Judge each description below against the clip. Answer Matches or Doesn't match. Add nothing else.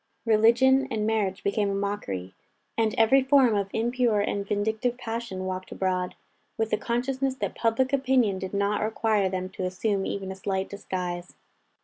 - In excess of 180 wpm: Doesn't match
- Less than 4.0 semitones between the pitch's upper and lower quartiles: Matches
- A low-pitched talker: Doesn't match